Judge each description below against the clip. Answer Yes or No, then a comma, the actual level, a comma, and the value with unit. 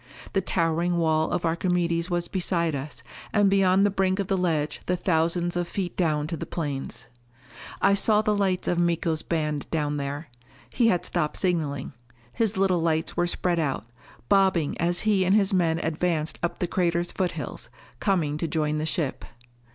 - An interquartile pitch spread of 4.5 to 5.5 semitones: No, average, 2.9 semitones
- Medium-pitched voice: Yes, medium, 170 Hz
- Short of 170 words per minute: No, average, 175 wpm